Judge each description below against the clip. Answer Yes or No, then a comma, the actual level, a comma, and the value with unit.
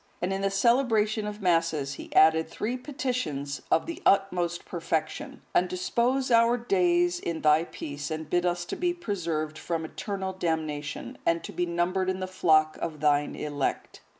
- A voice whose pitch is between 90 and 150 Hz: No, medium, 175 Hz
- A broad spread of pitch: Yes, wide, 6.2 semitones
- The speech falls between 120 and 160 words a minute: No, average, 170 wpm